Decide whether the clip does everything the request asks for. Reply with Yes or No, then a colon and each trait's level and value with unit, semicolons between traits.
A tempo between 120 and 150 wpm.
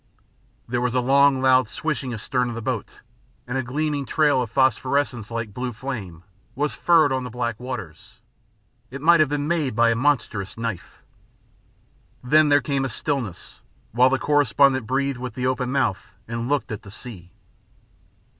No: average, 170 wpm